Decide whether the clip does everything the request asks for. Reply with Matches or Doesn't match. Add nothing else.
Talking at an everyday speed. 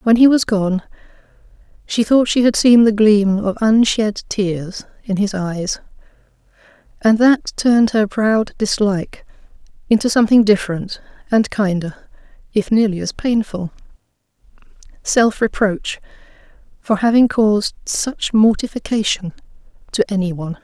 Doesn't match